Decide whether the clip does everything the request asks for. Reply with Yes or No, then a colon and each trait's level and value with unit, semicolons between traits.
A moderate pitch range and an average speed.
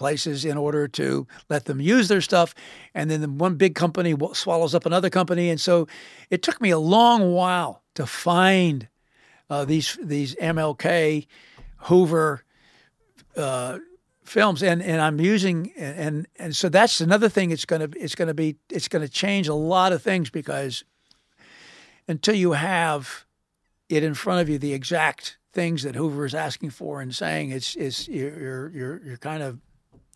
Yes: average, 3.7 semitones; average, 165 wpm